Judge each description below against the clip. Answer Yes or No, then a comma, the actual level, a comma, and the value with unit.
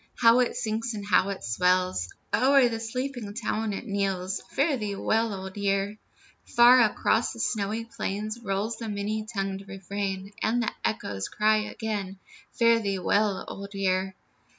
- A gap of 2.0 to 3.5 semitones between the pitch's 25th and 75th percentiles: Yes, narrow, 2.6 semitones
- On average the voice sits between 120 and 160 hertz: No, high, 205 Hz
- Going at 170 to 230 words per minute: No, average, 155 wpm